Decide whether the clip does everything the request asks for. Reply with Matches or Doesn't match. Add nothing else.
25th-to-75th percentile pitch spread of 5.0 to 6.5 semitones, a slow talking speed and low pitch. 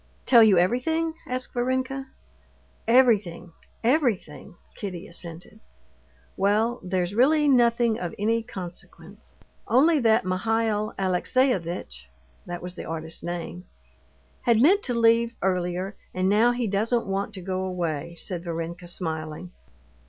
Doesn't match